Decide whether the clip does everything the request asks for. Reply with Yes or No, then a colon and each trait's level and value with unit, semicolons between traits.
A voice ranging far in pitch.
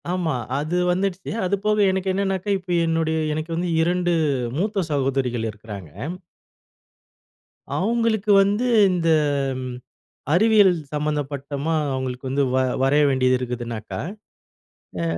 Yes: wide, 6.3 semitones